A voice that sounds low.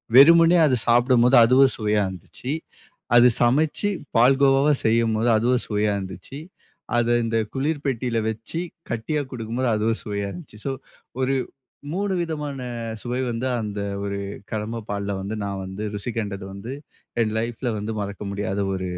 Yes: low, 115 Hz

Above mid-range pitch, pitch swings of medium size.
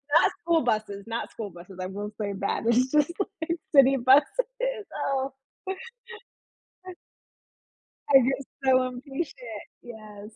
Yes: very high, 250 Hz; average, 4.7 semitones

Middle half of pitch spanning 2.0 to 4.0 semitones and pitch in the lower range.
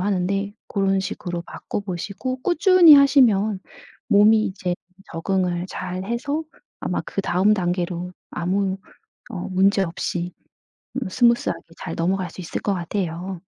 No: average, 3.0 semitones; high, 195 Hz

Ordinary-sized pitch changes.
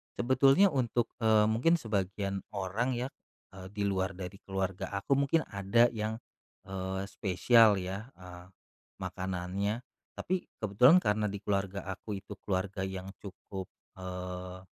Yes: average, 3.2 semitones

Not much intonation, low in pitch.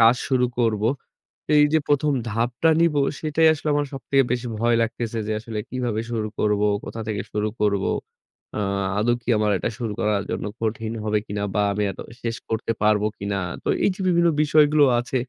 No: average, 4.3 semitones; low, 115 Hz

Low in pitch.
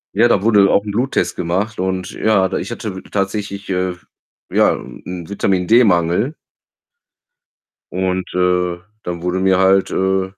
Yes: very low, 95 Hz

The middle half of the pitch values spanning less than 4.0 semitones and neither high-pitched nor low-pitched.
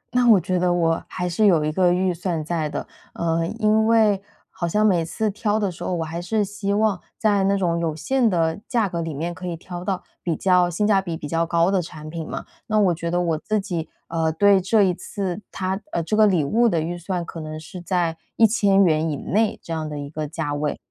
Yes: average, 3.6 semitones; medium, 175 Hz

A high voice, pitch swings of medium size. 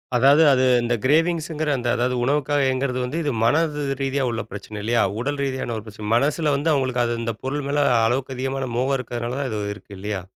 No: low, 130 Hz; average, 3.4 semitones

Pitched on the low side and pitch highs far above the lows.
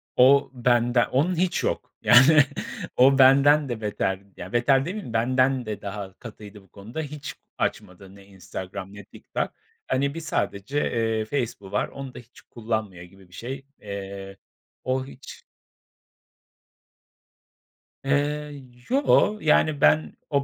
Yes: low, 120 Hz; wide, 5.7 semitones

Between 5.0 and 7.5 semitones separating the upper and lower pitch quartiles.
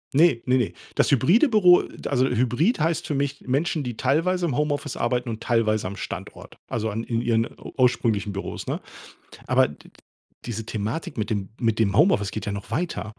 Yes: wide, 5.4 semitones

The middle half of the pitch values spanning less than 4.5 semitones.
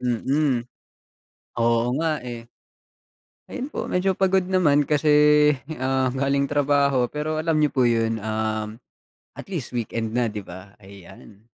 No: average, 4.9 semitones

